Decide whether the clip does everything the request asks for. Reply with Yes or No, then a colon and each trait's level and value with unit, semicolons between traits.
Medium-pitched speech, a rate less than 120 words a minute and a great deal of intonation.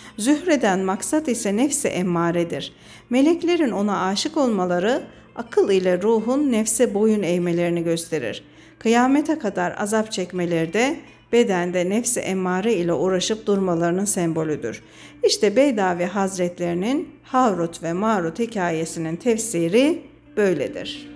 No: high, 200 Hz; average, 105 wpm; wide, 6.2 semitones